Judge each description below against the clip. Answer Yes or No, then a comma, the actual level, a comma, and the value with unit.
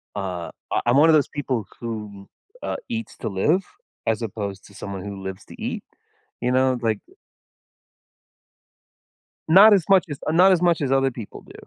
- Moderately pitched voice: No, low, 125 Hz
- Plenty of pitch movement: Yes, wide, 7.8 semitones